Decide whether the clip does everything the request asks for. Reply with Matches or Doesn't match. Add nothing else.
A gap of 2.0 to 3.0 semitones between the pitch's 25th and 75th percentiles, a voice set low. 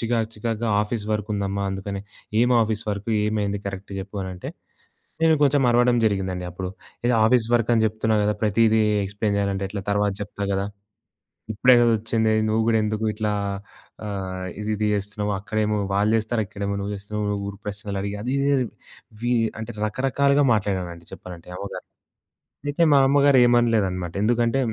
Matches